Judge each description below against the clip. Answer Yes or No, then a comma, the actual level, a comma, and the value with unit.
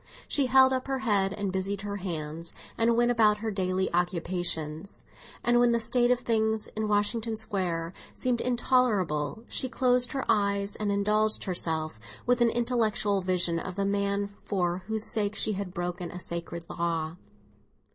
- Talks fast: No, average, 165 wpm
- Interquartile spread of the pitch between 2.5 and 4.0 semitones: No, average, 4.4 semitones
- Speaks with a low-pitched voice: No, high, 200 Hz